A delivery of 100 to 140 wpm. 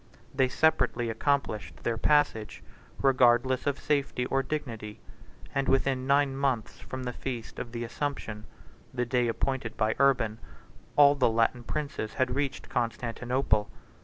Yes: slow, 135 wpm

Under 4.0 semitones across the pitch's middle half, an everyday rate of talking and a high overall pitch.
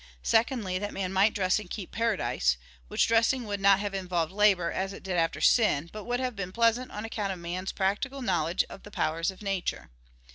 No: average, 3.4 semitones; fast, 210 wpm; high, 195 Hz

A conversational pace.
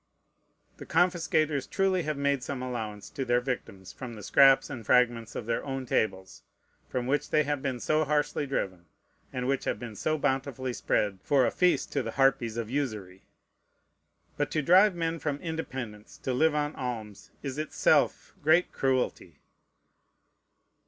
Yes: average, 160 wpm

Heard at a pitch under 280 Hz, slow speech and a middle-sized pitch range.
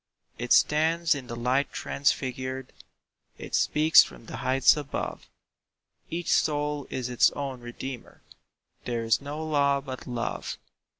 Yes: low, 135 Hz; slow, 130 wpm; average, 3.0 semitones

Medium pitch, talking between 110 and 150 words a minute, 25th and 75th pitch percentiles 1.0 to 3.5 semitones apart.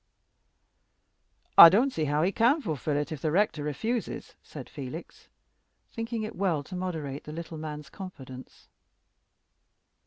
No: medium, 160 Hz; slow, 135 wpm; average, 5.2 semitones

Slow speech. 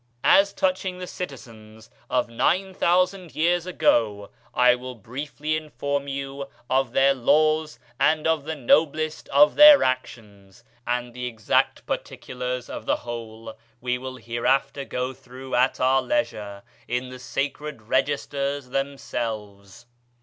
Yes: slow, 130 wpm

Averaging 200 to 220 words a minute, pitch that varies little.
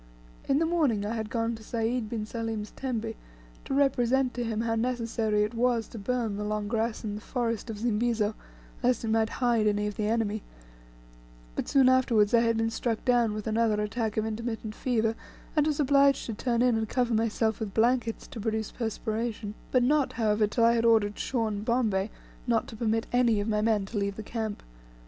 Yes: fast, 205 wpm; narrow, 2.1 semitones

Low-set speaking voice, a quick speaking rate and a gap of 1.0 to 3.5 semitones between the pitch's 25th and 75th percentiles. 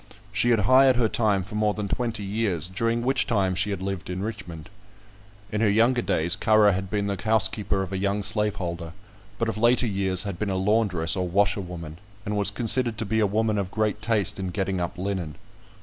Yes: low, 100 Hz; fast, 210 wpm; average, 2.8 semitones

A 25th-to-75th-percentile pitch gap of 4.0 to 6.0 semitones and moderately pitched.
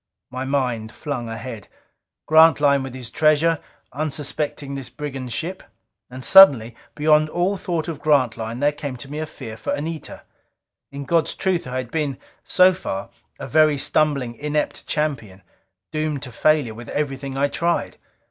No: average, 3.4 semitones; medium, 145 Hz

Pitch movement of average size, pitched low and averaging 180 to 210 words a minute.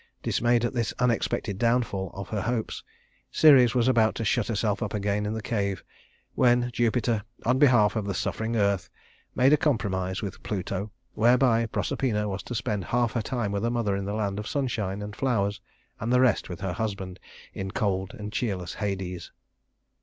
Yes: average, 3.2 semitones; low, 110 Hz; average, 185 wpm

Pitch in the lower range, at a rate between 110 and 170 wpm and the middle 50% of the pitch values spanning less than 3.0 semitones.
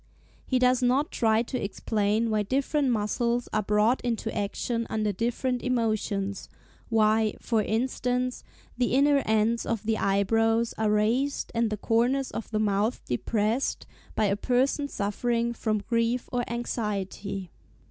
No: high, 225 Hz; average, 140 wpm; narrow, 2.6 semitones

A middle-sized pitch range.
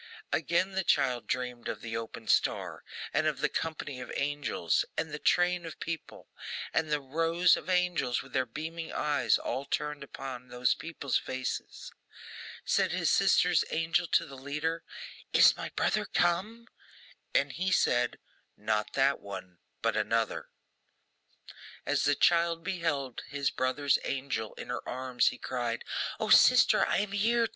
Yes: average, 4.9 semitones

